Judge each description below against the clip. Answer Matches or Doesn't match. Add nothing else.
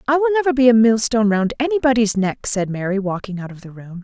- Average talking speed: Doesn't match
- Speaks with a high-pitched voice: Matches